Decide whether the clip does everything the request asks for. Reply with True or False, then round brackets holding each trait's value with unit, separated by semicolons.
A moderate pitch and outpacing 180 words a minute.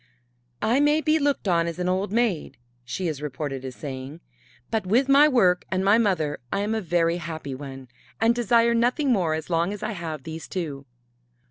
True (180 Hz; 200 wpm)